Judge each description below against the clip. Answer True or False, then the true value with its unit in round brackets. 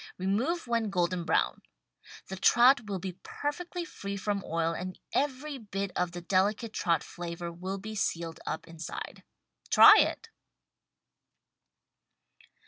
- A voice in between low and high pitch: False (195 Hz)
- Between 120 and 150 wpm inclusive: True (135 wpm)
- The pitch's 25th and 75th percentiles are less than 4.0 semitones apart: False (5.1 semitones)